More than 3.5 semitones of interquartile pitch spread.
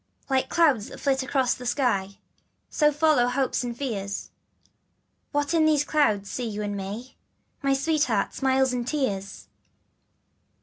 Yes: average, 5.1 semitones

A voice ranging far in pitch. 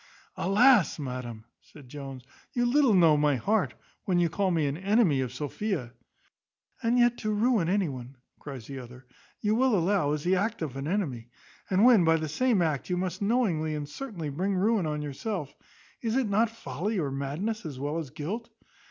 Yes: wide, 6.8 semitones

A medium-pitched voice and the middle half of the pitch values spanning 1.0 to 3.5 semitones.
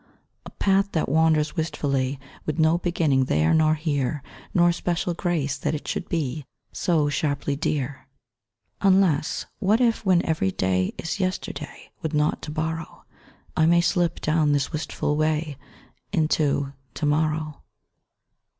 Yes: medium, 155 Hz; average, 2.8 semitones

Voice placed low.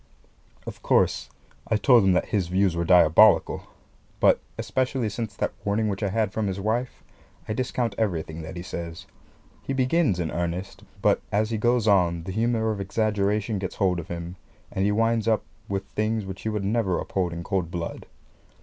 Yes: low, 100 Hz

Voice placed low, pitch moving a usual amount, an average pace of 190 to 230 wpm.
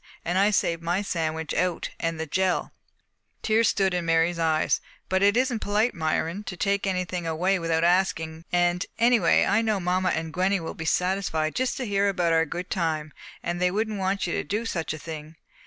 No: medium, 180 Hz; average, 3.3 semitones; average, 200 wpm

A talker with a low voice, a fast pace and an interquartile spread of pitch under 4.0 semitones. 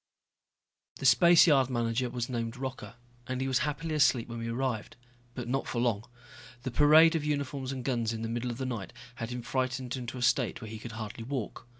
Yes: low, 125 Hz; fast, 210 wpm; narrow, 2.5 semitones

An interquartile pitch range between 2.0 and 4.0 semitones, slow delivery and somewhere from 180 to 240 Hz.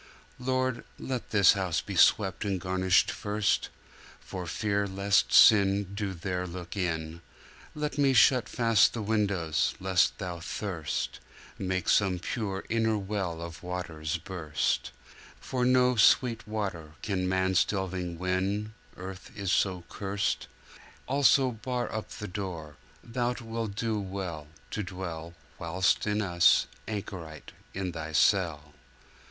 No: average, 3.2 semitones; slow, 130 wpm; very low, 95 Hz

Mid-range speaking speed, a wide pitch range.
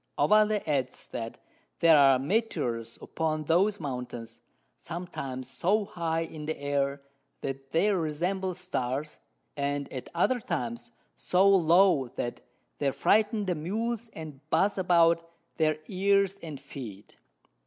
No: slow, 125 wpm; wide, 5.7 semitones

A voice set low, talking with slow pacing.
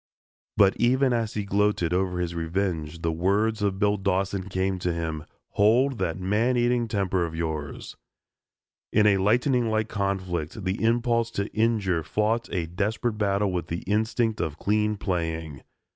No: low, 100 Hz; average, 160 wpm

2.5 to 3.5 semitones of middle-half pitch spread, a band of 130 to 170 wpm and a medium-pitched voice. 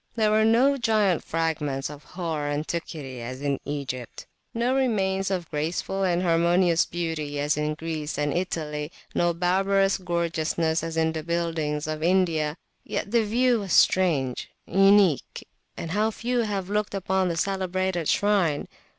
No: average, 4.2 semitones; average, 145 wpm; medium, 170 Hz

